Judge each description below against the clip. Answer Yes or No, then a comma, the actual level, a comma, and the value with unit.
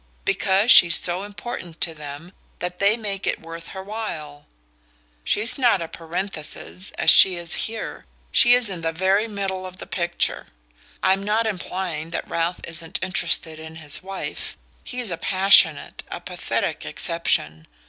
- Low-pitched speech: No, medium, 185 Hz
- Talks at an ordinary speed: Yes, average, 150 wpm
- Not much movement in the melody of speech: No, average, 3.3 semitones